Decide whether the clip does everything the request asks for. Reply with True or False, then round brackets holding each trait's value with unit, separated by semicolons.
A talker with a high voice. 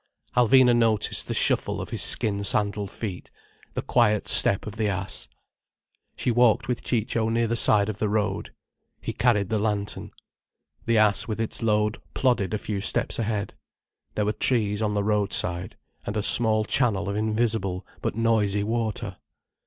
False (105 Hz)